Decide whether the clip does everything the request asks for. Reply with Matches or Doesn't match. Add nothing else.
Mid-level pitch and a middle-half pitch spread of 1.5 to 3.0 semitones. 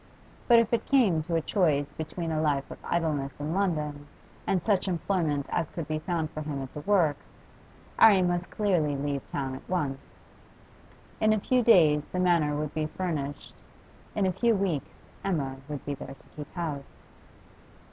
Doesn't match